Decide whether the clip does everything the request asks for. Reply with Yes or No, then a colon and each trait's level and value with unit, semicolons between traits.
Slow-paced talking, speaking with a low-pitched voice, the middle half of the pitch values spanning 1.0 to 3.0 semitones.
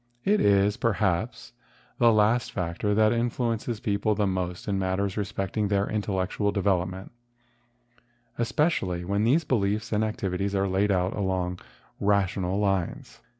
Yes: slow, 130 wpm; low, 100 Hz; narrow, 2.4 semitones